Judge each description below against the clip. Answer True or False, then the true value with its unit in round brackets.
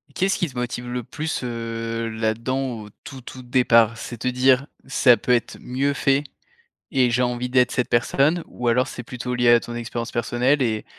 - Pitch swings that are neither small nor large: False (1.9 semitones)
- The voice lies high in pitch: False (125 Hz)